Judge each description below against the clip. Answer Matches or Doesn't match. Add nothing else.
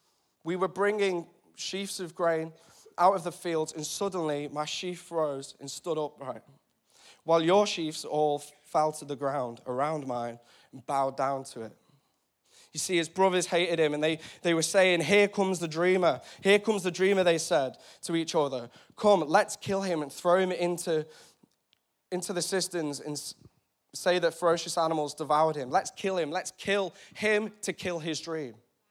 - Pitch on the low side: Doesn't match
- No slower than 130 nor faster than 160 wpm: Doesn't match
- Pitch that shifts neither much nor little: Matches